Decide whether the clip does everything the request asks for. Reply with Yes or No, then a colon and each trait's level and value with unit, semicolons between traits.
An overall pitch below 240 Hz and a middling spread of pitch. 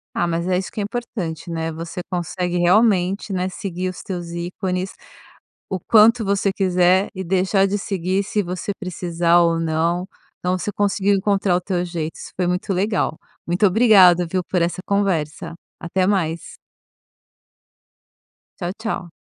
No: medium, 185 Hz; narrow, 2.2 semitones